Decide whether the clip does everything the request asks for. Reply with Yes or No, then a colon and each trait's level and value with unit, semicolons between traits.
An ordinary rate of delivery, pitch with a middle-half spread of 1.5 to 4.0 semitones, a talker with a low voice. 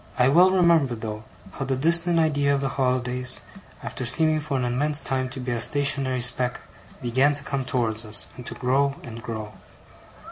Yes: average, 185 wpm; average, 2.8 semitones; low, 130 Hz